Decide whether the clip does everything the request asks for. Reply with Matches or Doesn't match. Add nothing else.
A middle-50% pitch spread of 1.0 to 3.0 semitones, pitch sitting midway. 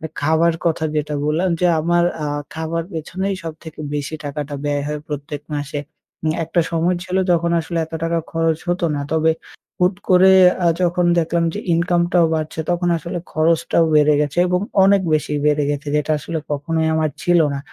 Matches